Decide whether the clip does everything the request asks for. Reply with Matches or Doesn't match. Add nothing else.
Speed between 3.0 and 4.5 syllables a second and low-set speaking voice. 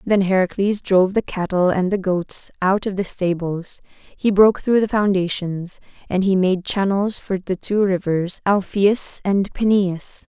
Doesn't match